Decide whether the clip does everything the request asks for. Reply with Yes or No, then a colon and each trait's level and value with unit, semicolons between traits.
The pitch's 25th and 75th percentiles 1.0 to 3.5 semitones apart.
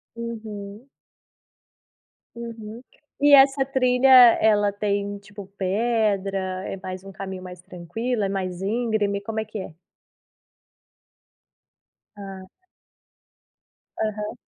Yes: average, 3.1 semitones